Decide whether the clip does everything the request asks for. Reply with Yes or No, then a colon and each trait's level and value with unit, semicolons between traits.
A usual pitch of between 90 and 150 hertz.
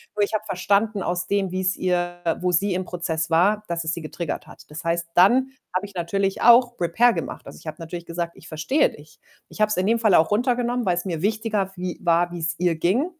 No: medium, 180 Hz